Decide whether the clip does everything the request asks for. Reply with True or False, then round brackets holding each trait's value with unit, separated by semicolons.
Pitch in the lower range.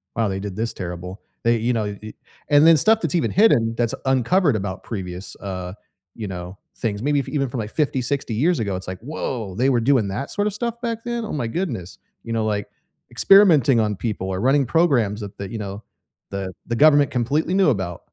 True (115 Hz)